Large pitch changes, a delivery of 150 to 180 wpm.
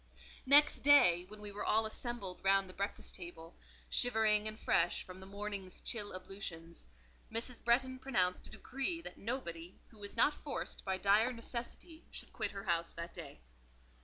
No: average, 4.4 semitones; average, 165 wpm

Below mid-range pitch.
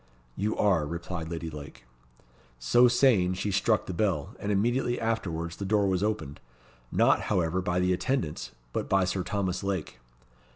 Yes: very low, 95 Hz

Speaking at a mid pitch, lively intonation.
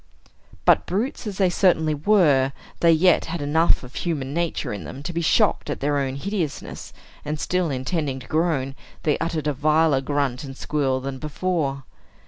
No: medium, 150 Hz; average, 3.8 semitones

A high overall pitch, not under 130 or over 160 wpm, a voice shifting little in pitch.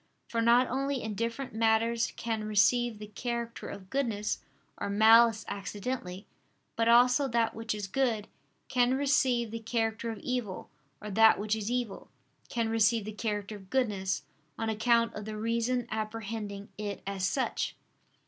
Yes: high, 225 Hz; average, 150 wpm; narrow, 2.1 semitones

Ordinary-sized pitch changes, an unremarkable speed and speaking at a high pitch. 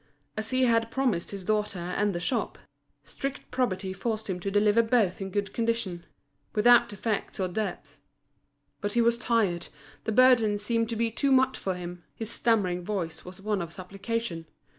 Yes: average, 3.8 semitones; average, 175 wpm; high, 210 Hz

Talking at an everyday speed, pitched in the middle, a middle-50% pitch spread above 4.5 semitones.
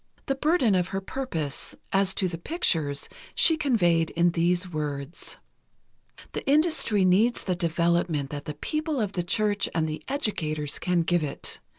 Yes: average, 160 wpm; medium, 180 Hz; average, 5.2 semitones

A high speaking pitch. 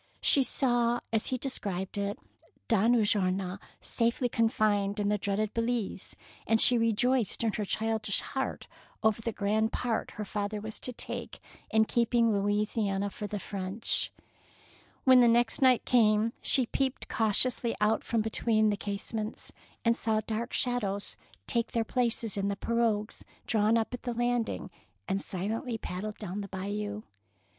Yes: high, 220 Hz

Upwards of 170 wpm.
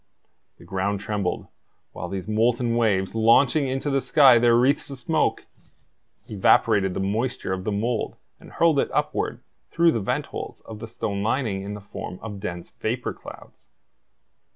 No: average, 165 wpm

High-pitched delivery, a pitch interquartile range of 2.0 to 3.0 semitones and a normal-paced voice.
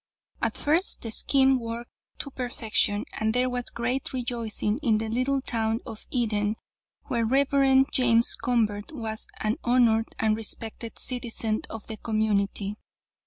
Yes: high, 230 Hz; narrow, 2.4 semitones; average, 145 wpm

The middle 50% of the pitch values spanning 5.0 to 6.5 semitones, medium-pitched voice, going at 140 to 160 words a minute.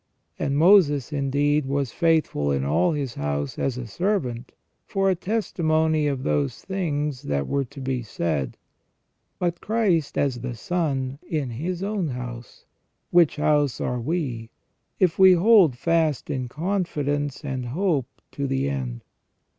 Yes: wide, 5.4 semitones; medium, 145 Hz; average, 145 wpm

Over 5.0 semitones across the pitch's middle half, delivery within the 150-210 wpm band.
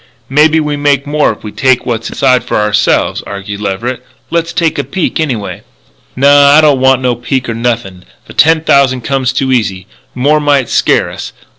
No: average, 3.8 semitones; average, 190 wpm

